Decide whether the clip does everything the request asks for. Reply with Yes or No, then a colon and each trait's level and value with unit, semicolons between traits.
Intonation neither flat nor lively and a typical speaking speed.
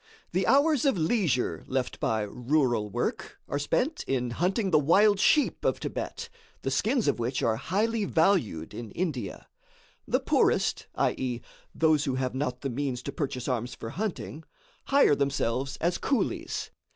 No: wide, 7.7 semitones; average, 155 wpm